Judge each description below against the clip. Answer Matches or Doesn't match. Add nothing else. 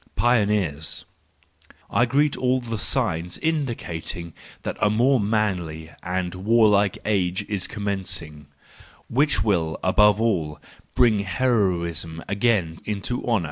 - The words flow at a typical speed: Doesn't match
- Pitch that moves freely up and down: Doesn't match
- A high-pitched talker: Doesn't match